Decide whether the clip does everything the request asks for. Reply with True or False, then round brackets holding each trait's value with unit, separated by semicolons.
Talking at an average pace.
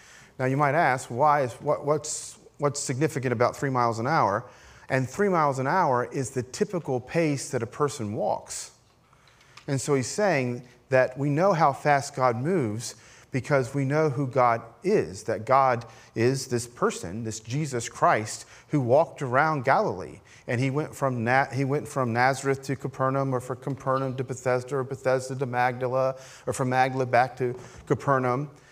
True (175 wpm)